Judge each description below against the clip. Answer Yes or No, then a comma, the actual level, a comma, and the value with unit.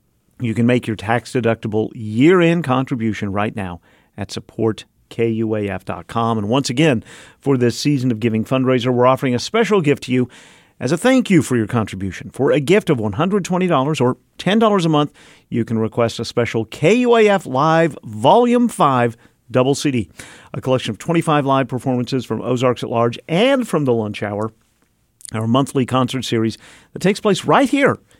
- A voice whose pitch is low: Yes, low, 125 Hz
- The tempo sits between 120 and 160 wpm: No, average, 170 wpm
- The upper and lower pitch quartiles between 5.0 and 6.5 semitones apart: Yes, wide, 5.6 semitones